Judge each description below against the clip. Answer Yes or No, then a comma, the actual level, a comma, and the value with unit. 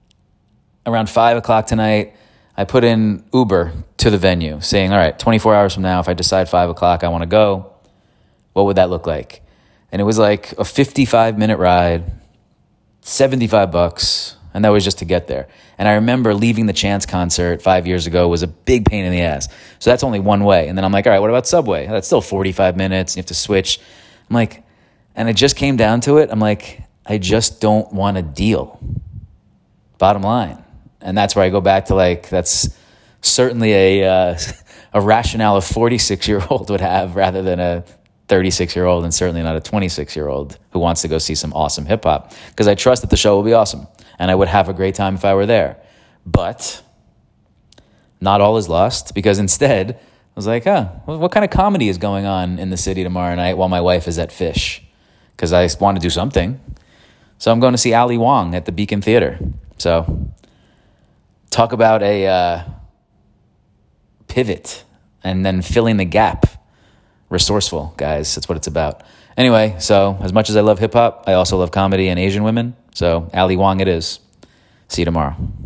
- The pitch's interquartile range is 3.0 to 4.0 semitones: Yes, average, 3.4 semitones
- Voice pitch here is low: Yes, very low, 95 Hz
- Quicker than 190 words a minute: Yes, fast, 205 wpm